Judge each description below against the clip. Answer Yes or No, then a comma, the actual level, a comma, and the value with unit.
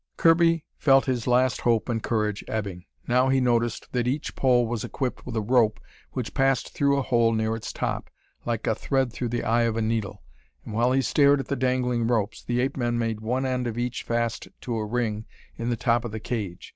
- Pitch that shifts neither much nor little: No, narrow, 2.3 semitones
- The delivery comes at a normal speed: No, fast, 220 wpm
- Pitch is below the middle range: Yes, low, 120 Hz